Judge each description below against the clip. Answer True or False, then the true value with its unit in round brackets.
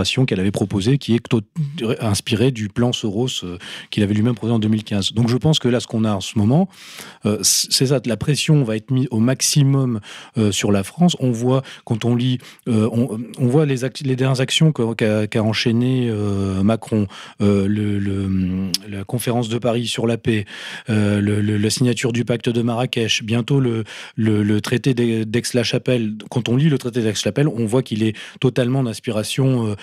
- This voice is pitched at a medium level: False (115 Hz)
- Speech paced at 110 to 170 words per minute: False (195 wpm)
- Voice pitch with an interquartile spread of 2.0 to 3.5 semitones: True (3.2 semitones)